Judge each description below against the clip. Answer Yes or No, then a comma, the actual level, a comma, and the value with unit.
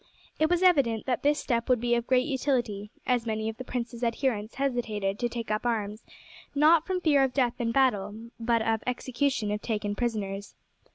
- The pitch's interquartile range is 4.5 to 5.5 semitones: No, average, 3.4 semitones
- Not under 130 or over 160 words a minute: No, average, 190 wpm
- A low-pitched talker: No, high, 240 Hz